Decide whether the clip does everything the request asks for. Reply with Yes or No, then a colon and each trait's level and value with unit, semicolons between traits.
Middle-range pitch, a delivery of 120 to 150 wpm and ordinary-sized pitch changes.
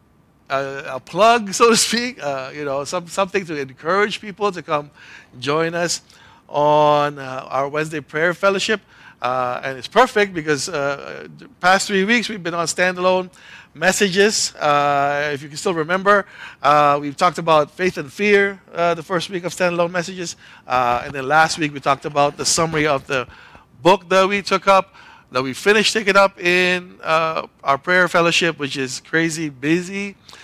No: medium, 170 Hz; average, 175 wpm; average, 4.9 semitones